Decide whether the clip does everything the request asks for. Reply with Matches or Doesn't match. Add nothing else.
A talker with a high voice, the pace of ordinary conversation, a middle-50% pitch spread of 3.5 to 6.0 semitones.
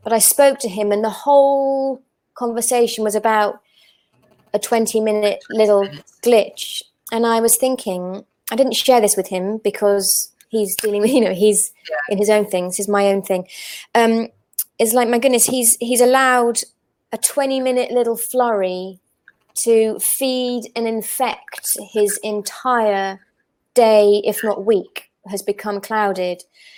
Doesn't match